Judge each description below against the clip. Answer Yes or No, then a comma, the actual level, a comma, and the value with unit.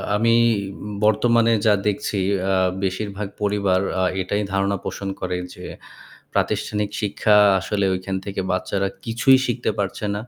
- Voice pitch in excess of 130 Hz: No, low, 100 Hz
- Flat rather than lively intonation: Yes, narrow, 1.7 semitones